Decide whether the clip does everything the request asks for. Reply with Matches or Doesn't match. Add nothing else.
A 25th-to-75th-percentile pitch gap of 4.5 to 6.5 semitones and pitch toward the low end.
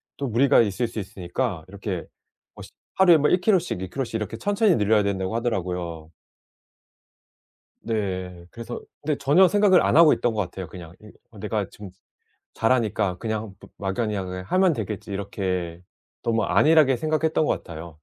Doesn't match